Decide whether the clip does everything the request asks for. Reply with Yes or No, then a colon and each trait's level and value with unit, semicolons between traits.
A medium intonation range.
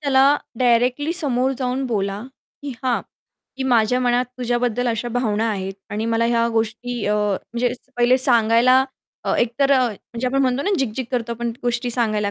No: narrow, 2.0 semitones